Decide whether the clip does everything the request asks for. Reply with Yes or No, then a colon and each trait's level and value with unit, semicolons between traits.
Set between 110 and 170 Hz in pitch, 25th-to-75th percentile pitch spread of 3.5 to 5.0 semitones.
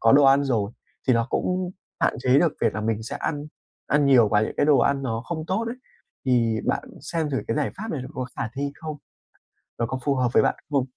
Yes: low, 135 Hz; average, 4.2 semitones